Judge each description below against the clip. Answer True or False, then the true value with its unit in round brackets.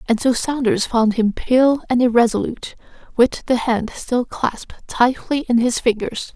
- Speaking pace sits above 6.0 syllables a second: False (4.5 syllables/s)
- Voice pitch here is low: False (240 Hz)